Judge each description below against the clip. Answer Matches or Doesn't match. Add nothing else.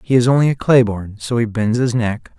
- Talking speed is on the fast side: Matches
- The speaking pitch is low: Matches